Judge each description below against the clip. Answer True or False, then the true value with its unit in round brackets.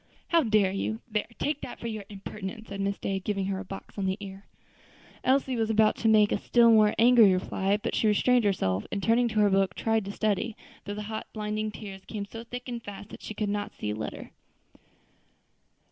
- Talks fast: True (220 wpm)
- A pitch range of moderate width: False (2.2 semitones)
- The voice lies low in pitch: False (210 Hz)